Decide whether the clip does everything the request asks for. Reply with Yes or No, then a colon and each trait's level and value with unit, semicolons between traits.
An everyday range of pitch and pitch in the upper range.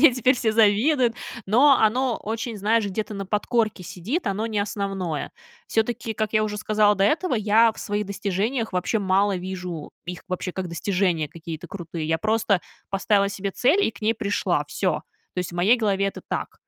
Yes: average, 3.0 semitones; high, 205 Hz